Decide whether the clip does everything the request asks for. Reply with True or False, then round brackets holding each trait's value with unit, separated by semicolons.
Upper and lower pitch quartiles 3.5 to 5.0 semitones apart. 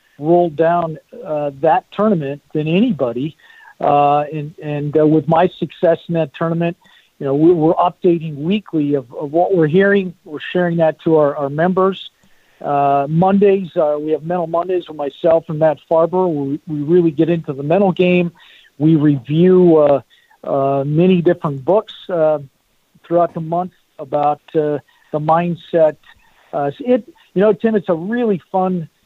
False (3.1 semitones)